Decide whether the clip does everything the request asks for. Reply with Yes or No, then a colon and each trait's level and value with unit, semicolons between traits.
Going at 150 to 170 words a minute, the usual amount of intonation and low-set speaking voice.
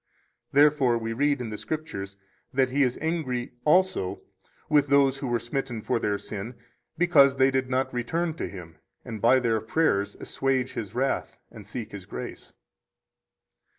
Yes: average, 160 wpm; average, 3.9 semitones; low, 130 Hz